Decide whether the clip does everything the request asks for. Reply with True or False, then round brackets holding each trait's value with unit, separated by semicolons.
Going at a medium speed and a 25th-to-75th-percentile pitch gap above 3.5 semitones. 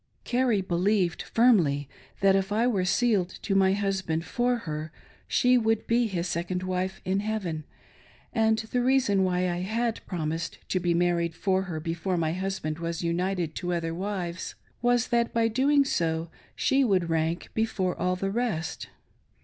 True (165 wpm; 4.4 semitones)